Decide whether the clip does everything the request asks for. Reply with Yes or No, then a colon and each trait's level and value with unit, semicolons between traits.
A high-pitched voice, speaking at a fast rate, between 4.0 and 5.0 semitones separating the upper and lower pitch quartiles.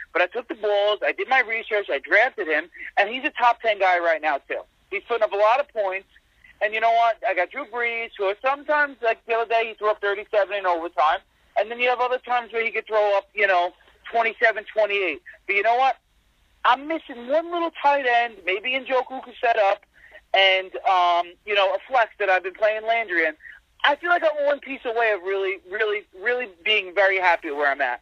Yes: high, 225 Hz; fast, 230 wpm; average, 4.3 semitones